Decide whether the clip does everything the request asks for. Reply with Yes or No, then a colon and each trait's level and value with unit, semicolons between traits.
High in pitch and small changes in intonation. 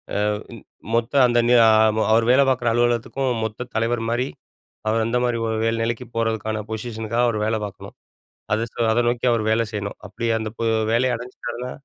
No: low, 115 Hz; narrow, 1.5 semitones